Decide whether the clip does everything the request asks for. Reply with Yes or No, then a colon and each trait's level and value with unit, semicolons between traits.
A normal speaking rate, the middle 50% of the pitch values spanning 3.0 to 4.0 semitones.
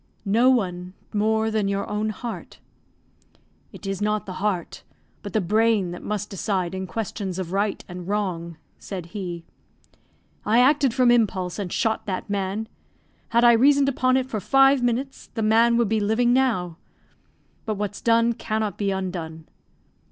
Yes: average, 160 wpm; average, 3.6 semitones